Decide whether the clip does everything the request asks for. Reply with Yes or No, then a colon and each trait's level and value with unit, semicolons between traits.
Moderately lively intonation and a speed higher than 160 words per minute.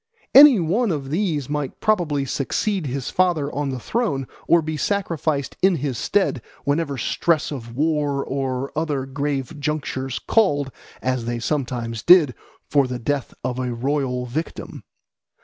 No: average, 3.7 semitones; average, 150 wpm